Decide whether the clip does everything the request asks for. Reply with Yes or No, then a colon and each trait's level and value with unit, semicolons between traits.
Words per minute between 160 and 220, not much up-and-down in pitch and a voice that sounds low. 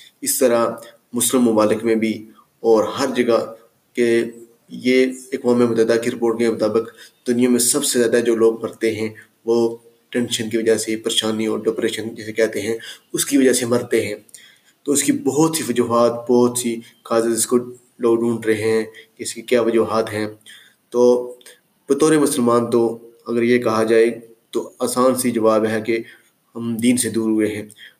Yes: average, 180 wpm; narrow, 1.5 semitones; low, 115 Hz